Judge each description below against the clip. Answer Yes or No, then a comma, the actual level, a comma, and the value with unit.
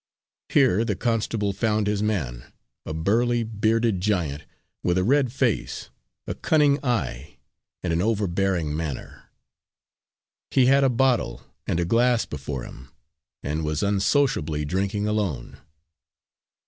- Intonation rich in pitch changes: Yes, wide, 6.2 semitones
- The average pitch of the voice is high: No, low, 105 Hz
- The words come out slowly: Yes, slow, 125 wpm